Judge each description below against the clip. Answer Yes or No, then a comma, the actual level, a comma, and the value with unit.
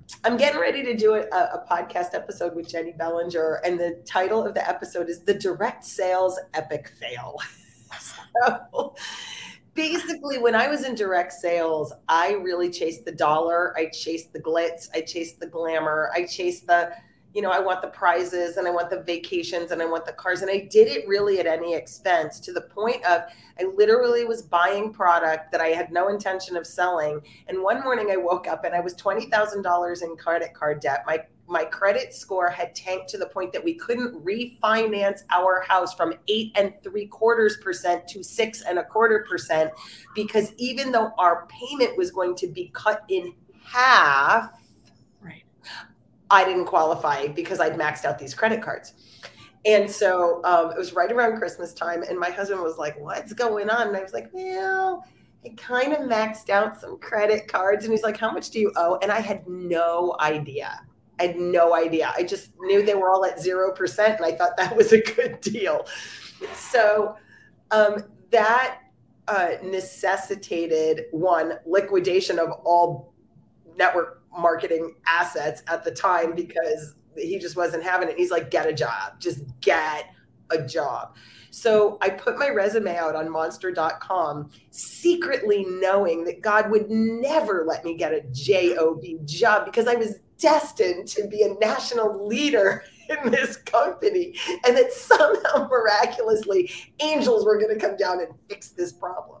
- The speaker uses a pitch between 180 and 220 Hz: Yes, medium, 185 Hz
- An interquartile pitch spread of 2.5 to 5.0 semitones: Yes, average, 4.6 semitones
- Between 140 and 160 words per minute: No, average, 175 wpm